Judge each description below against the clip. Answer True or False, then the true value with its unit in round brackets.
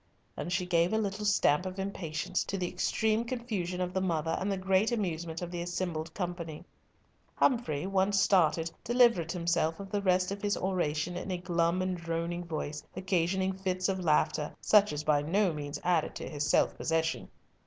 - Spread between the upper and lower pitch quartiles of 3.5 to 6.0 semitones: False (2.8 semitones)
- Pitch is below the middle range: False (180 Hz)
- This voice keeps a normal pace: True (185 wpm)